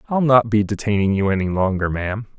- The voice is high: No, low, 105 Hz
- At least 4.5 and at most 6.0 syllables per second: No, 6.2 syllables/s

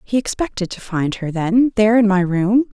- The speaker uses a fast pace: Yes, fast, 215 wpm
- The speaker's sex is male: No, female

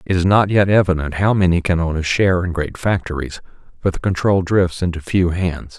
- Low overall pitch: Yes, very low, 90 Hz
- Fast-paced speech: Yes, fast, 220 wpm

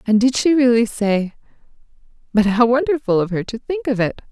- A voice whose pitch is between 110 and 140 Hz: No, high, 230 Hz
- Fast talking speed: No, average, 180 wpm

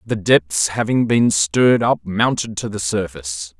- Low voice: Yes, low, 100 Hz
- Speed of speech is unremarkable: Yes, average, 165 wpm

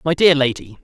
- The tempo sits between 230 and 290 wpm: No, fast, 215 wpm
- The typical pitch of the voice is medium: Yes, medium, 145 Hz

